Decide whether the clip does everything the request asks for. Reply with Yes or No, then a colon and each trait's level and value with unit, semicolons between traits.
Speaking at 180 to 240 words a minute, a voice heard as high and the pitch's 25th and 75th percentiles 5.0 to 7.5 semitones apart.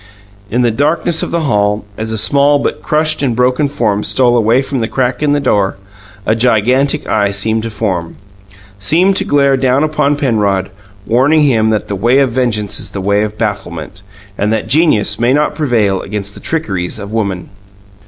No: average, 190 wpm; low, 115 Hz; average, 5.3 semitones